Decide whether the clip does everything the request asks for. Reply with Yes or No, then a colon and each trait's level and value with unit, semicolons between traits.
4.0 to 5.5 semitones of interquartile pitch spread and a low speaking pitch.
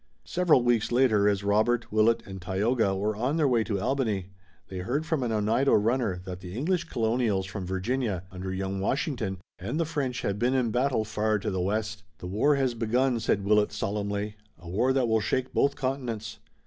Yes: average, 4.4 semitones; low, 110 Hz